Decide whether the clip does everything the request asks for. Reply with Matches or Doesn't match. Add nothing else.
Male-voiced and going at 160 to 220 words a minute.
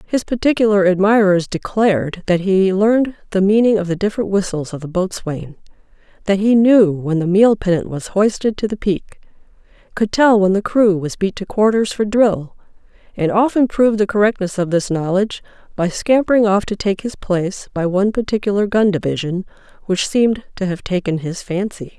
Doesn't match